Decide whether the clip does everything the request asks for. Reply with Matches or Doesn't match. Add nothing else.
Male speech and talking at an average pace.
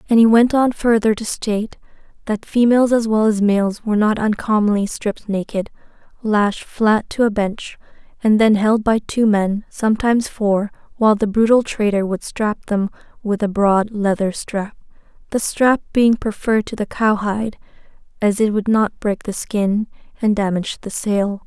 Doesn't match